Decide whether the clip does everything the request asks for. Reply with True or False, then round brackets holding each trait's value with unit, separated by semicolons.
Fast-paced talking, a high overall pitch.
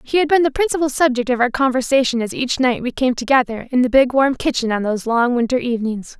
True (240 wpm; 255 Hz)